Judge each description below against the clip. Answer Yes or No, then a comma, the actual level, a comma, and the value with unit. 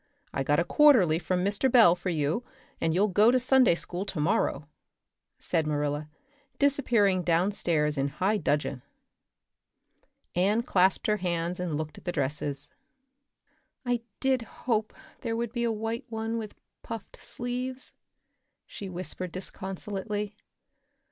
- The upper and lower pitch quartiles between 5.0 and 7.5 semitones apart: Yes, wide, 5.6 semitones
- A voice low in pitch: No, high, 190 Hz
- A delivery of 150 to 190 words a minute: No, slow, 135 wpm